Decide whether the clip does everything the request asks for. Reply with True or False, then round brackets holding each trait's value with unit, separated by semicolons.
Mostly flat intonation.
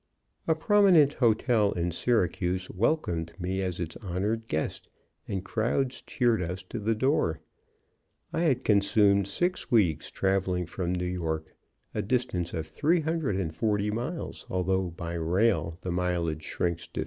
False (5.3 semitones)